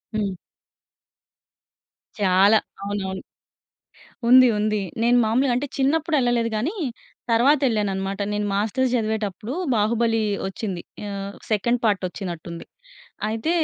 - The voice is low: No, high, 215 Hz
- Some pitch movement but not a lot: Yes, average, 3.5 semitones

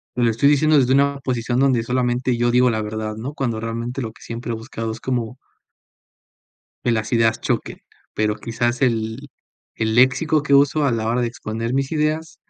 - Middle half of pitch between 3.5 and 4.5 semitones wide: No, average, 3.0 semitones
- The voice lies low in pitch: Yes, low, 120 Hz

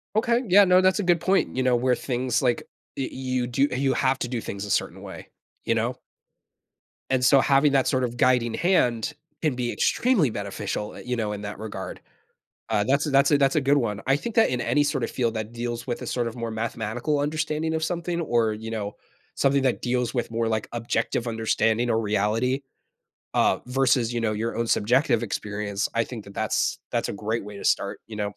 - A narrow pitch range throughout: No, average, 3.6 semitones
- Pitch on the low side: Yes, low, 120 Hz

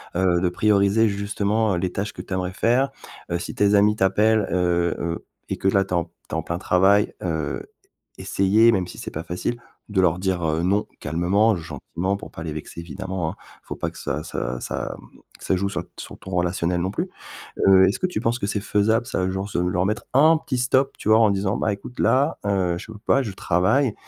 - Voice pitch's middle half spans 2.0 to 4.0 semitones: Yes, average, 3.3 semitones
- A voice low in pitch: Yes, very low, 95 Hz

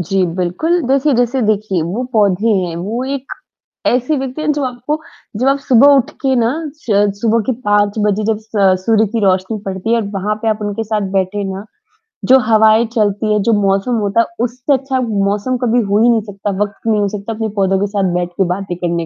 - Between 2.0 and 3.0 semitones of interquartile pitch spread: No, average, 3.5 semitones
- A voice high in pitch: Yes, high, 215 Hz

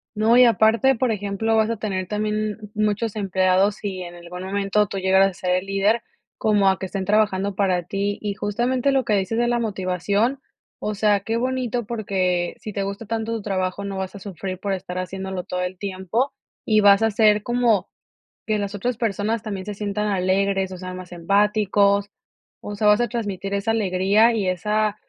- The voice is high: Yes, high, 200 Hz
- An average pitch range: No, narrow, 2.3 semitones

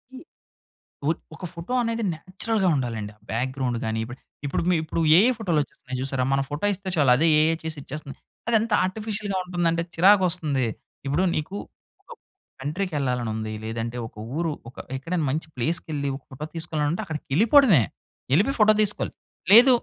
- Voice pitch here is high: No, medium, 160 Hz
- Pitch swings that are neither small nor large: No, wide, 6.2 semitones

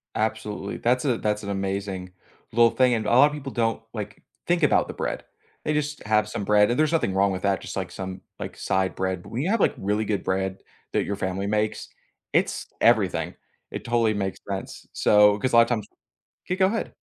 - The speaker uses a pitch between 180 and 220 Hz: No, low, 105 Hz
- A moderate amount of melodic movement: Yes, average, 3.7 semitones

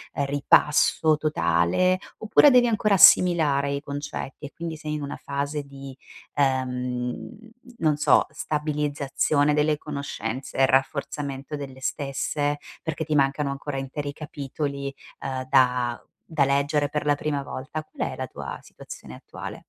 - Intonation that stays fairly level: Yes, narrow, 1.9 semitones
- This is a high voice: No, medium, 145 Hz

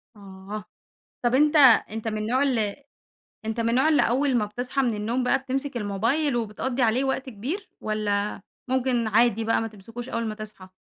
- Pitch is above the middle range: Yes, high, 230 Hz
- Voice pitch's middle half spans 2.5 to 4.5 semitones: Yes, average, 3.5 semitones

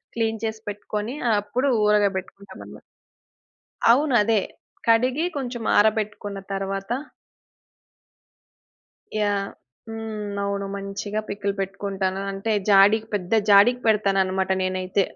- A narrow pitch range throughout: Yes, narrow, 2.1 semitones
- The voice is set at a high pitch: Yes, high, 205 Hz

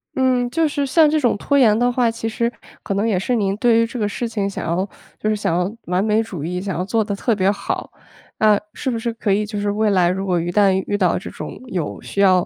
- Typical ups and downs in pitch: Yes, average, 3.4 semitones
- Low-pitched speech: No, high, 210 Hz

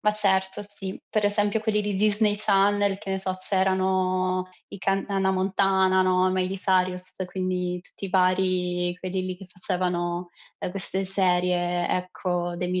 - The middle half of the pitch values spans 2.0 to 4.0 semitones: No, narrow, 1.2 semitones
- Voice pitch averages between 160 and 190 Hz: Yes, medium, 185 Hz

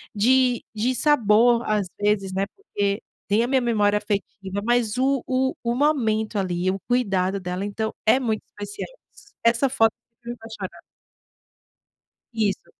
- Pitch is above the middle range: Yes, high, 220 Hz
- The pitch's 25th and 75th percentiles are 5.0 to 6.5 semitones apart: No, average, 3.3 semitones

